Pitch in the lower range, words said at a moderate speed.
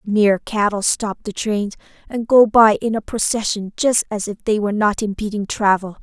No: high, 210 Hz; average, 190 wpm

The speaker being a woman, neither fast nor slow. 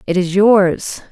Yes: female; average, 160 wpm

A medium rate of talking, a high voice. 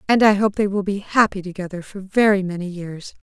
No: fast, 220 wpm; high, 195 Hz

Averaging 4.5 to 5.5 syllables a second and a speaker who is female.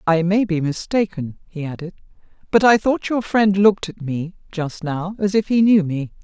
Yes: 4.8 syllables/s; female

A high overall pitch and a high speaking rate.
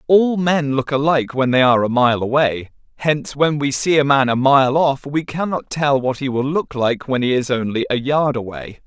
No: low, 135 Hz; fast, 230 wpm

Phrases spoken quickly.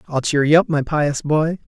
Yes: fast, 240 wpm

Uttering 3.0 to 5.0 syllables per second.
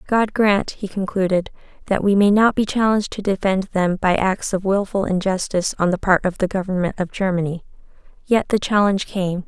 No: 5.4 syllables/s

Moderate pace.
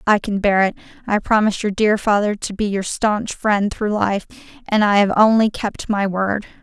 No: fast, 210 wpm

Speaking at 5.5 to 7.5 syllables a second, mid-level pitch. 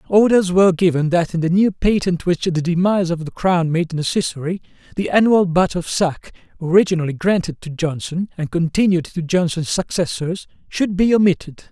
No: 5.3 syllables/s; medium, 175 Hz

